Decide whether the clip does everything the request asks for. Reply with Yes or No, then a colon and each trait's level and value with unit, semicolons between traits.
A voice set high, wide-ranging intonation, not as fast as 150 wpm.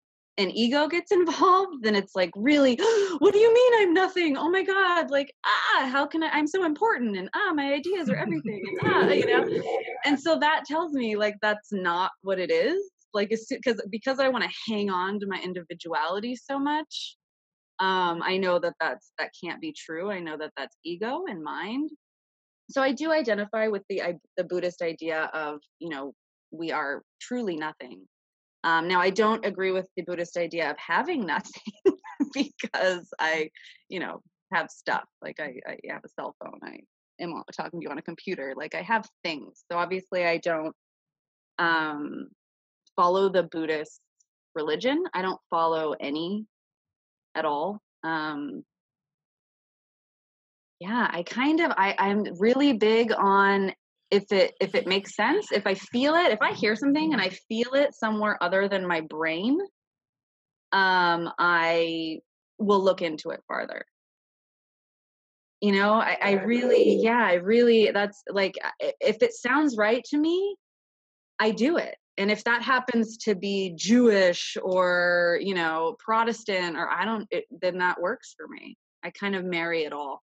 No: high, 210 Hz; wide, 7.9 semitones; average, 170 wpm